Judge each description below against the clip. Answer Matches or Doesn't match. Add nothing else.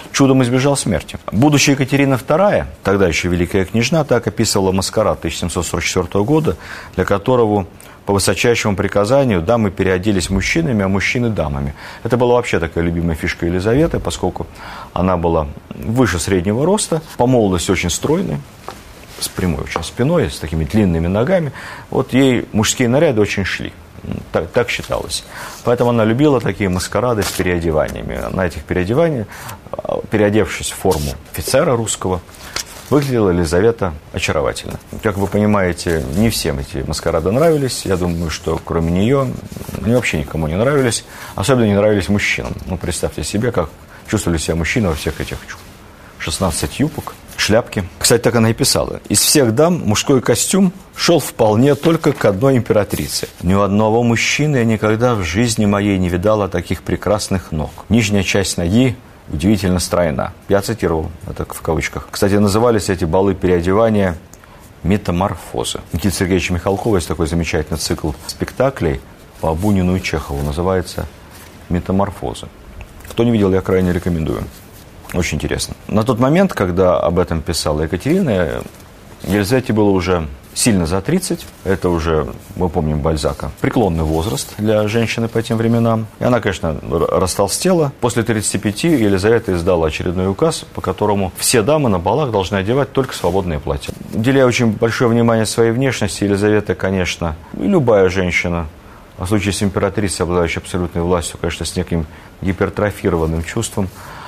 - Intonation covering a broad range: Doesn't match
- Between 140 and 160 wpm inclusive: Matches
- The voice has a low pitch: Matches